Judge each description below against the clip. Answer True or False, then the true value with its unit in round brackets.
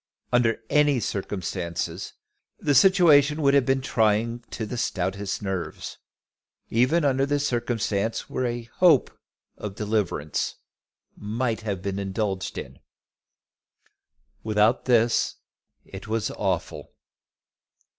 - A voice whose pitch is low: True (115 Hz)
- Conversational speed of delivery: False (105 wpm)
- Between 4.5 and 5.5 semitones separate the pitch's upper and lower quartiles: True (4.8 semitones)